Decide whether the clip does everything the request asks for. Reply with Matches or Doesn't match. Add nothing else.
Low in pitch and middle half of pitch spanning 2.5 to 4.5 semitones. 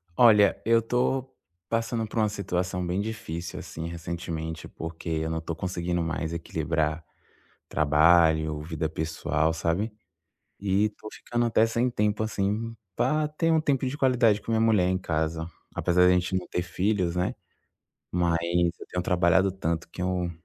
Doesn't match